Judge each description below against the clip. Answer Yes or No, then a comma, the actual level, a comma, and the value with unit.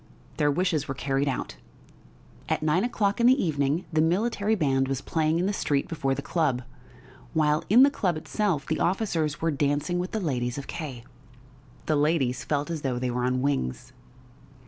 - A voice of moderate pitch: Yes, medium, 155 Hz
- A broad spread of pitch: No, average, 4.6 semitones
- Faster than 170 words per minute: Yes, average, 185 wpm